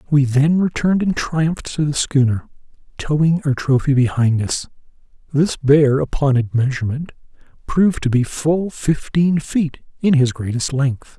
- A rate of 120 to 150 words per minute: Yes, average, 145 wpm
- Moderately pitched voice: Yes, medium, 145 Hz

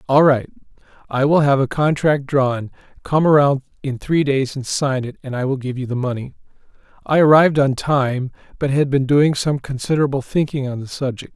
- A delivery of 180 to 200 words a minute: Yes, average, 195 wpm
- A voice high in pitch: No, low, 135 Hz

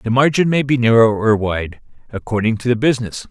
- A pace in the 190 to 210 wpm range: Yes, average, 200 wpm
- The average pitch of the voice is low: Yes, low, 120 Hz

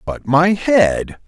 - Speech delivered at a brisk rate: No, average, 140 wpm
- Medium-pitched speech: Yes, medium, 155 Hz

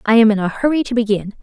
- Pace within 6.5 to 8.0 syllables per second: Yes, 7.1 syllables/s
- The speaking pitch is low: No, high, 225 Hz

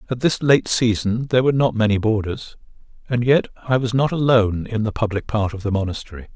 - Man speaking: Yes, male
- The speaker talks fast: Yes, fast, 210 wpm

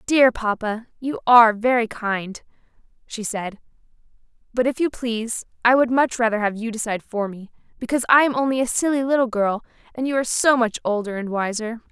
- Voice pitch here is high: Yes, high, 235 Hz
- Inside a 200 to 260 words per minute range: No, average, 185 wpm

